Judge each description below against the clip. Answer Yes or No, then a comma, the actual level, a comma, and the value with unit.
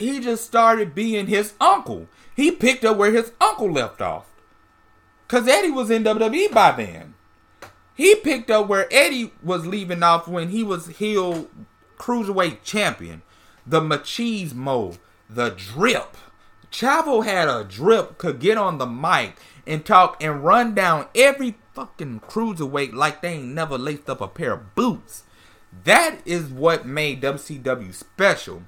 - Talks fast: No, average, 150 wpm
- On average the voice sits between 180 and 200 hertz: Yes, medium, 185 Hz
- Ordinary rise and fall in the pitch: No, wide, 7.9 semitones